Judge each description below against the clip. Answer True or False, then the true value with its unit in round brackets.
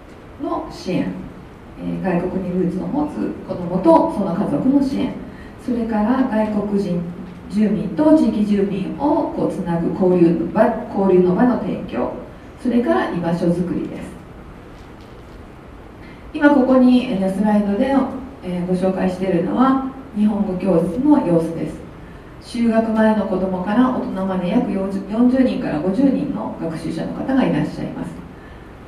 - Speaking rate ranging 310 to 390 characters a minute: False (265 characters per minute)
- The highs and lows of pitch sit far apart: True (5.8 semitones)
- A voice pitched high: True (210 Hz)